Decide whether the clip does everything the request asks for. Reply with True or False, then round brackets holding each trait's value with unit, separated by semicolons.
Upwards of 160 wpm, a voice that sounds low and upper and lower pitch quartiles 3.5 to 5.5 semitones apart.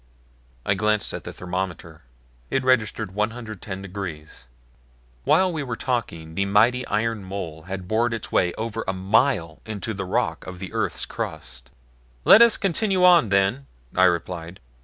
False (155 wpm; 100 Hz; 4.0 semitones)